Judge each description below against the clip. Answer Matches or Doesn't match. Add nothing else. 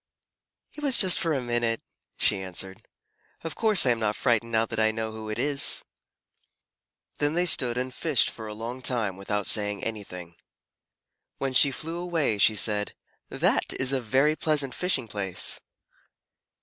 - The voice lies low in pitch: Matches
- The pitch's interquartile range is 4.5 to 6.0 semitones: Matches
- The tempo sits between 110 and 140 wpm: Doesn't match